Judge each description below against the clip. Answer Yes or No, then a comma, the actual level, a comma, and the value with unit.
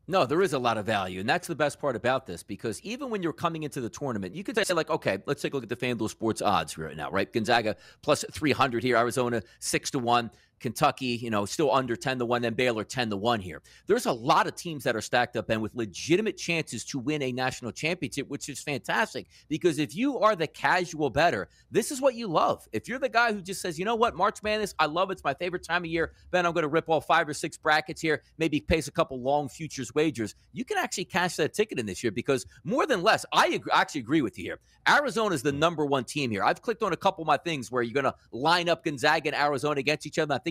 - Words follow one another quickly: Yes, fast, 270 wpm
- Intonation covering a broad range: Yes, wide, 5.7 semitones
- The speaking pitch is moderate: Yes, medium, 150 Hz